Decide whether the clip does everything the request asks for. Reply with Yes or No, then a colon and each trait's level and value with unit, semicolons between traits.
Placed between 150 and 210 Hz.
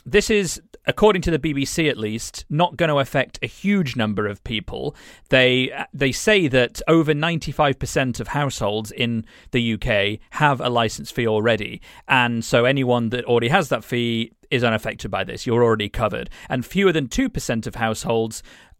No: low, 125 Hz